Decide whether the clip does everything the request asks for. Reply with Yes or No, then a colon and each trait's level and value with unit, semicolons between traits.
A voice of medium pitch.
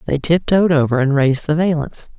Yes: medium, 155 Hz